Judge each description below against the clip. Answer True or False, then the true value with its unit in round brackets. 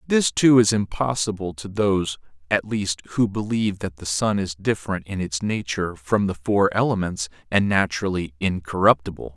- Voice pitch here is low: True (95 Hz)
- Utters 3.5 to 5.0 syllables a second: False (5.2 syllables/s)